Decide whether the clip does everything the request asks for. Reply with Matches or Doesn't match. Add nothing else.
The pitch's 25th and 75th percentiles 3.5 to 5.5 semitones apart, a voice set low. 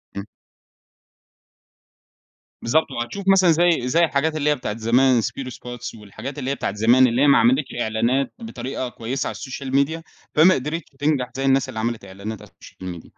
Matches